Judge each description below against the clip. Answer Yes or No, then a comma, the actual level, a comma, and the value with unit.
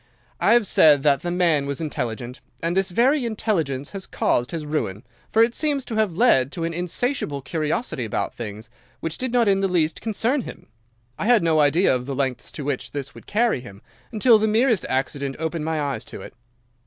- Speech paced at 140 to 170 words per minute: No, fast, 205 wpm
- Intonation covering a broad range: Yes, wide, 7.7 semitones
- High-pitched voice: No, medium, 165 Hz